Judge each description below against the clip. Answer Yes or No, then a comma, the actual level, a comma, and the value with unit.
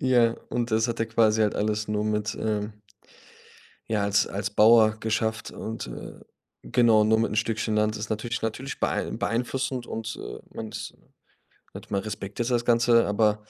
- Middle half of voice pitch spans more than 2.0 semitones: No, narrow, 1.6 semitones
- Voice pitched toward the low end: Yes, low, 110 Hz